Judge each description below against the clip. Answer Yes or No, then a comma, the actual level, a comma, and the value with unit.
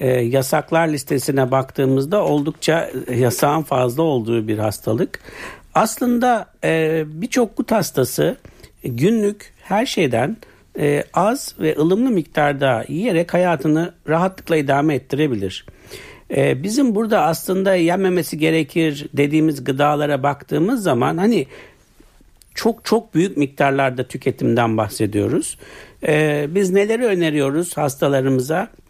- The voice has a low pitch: No, medium, 155 Hz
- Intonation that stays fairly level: No, average, 4.7 semitones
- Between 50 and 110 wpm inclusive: Yes, slow, 95 wpm